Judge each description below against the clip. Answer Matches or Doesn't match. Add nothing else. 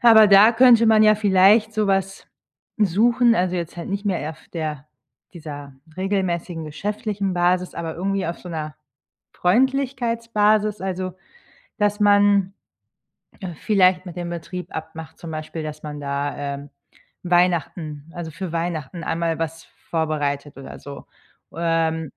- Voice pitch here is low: Doesn't match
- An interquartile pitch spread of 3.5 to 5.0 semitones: Matches